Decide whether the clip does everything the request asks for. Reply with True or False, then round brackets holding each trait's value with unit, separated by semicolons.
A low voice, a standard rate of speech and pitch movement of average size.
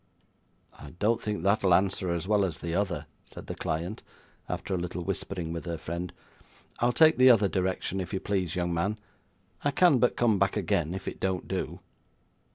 True (95 Hz; 190 wpm; 3.4 semitones)